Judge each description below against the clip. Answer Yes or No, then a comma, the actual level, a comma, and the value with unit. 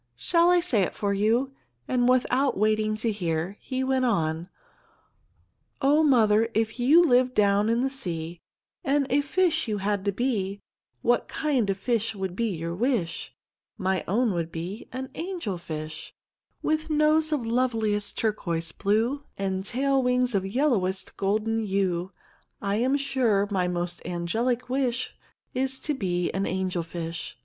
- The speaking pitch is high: Yes, high, 220 Hz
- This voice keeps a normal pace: Yes, average, 155 wpm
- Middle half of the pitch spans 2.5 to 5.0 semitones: No, wide, 5.4 semitones